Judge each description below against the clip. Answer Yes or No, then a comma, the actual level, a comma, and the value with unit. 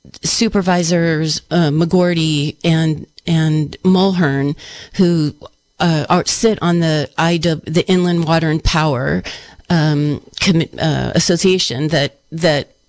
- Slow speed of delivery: Yes, slow, 110 wpm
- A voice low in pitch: No, medium, 165 Hz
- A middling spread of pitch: No, narrow, 2.3 semitones